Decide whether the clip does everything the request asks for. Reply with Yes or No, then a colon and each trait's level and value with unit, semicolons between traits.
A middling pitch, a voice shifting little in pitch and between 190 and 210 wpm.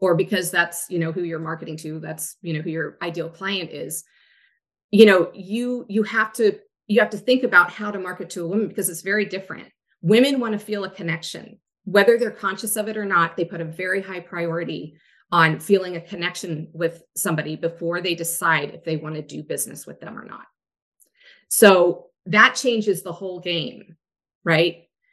No: medium, 180 Hz; average, 3.8 semitones; average, 200 wpm